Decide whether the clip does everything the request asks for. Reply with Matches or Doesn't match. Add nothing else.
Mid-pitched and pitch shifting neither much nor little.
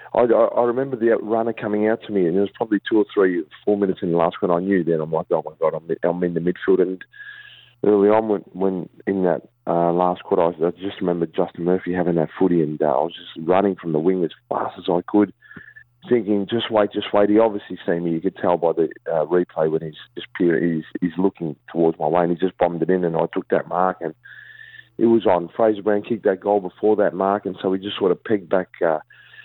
Doesn't match